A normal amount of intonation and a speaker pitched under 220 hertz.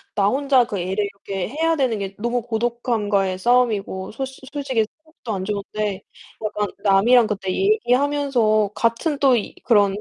No: average, 4.5 semitones; high, 225 Hz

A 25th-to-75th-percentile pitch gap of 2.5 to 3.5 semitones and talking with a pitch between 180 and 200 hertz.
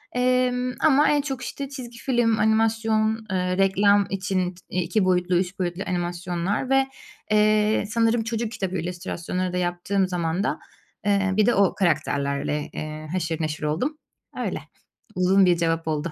No: average, 4.2 semitones; high, 190 Hz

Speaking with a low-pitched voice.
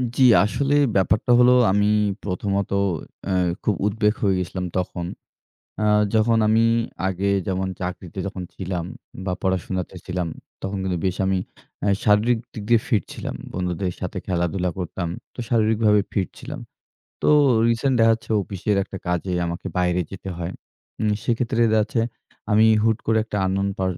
Yes: low, 100 Hz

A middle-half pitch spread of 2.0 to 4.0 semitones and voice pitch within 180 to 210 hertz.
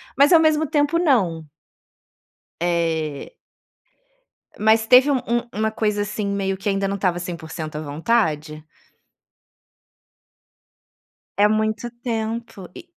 No: wide, 5.6 semitones; high, 205 Hz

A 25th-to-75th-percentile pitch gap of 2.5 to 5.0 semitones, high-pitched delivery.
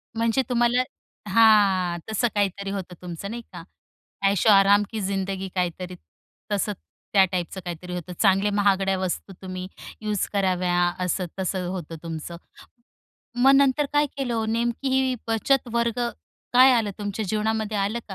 Yes: average, 3.6 semitones; high, 200 Hz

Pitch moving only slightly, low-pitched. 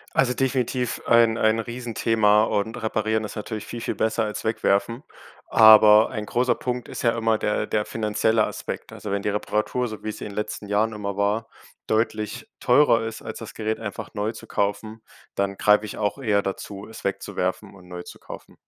Yes: narrow, 1.5 semitones; low, 110 Hz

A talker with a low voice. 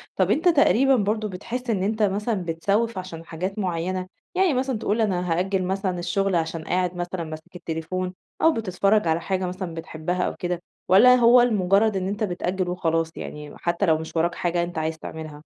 No: medium, 185 Hz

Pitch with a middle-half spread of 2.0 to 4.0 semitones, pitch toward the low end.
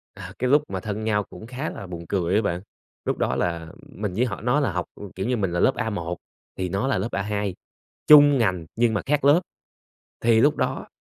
No: average, 5.3 semitones; low, 105 Hz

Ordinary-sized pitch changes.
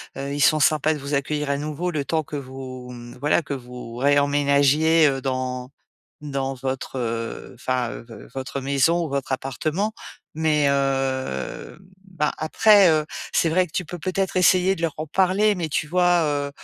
Yes: average, 3.2 semitones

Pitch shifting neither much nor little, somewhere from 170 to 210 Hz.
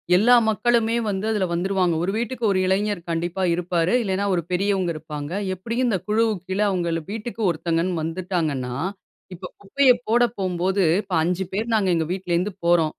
Yes: average, 3.5 semitones; high, 190 Hz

